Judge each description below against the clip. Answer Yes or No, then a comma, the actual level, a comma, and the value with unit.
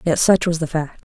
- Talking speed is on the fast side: Yes, fast, 280 wpm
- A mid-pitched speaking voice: Yes, medium, 165 Hz